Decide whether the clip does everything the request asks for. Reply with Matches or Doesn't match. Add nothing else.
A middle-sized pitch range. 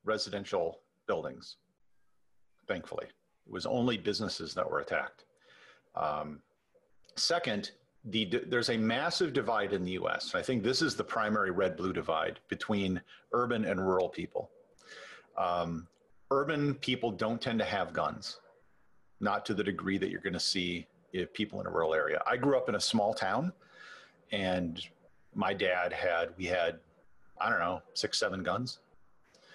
Matches